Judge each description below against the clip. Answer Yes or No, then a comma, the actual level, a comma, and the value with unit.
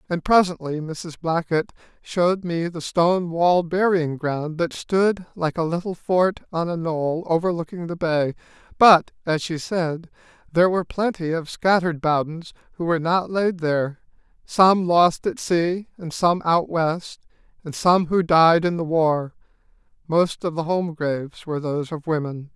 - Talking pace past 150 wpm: Yes, average, 160 wpm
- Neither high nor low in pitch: Yes, medium, 170 Hz